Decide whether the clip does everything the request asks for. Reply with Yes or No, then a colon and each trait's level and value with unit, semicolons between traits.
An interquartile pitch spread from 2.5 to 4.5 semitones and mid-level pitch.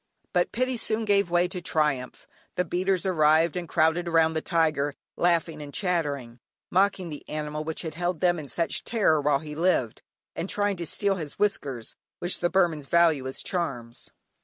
Yes: average, 3.2 semitones; medium, 165 Hz